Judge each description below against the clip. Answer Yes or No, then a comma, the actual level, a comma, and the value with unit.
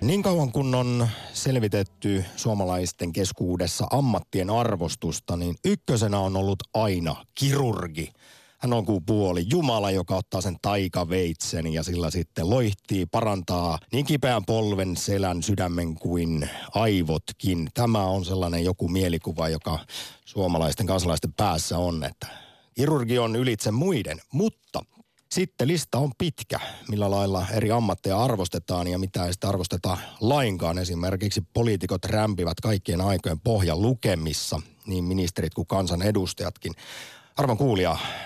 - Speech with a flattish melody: No, average, 4.8 semitones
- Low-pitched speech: Yes, very low, 95 Hz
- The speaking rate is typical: Yes, average, 125 wpm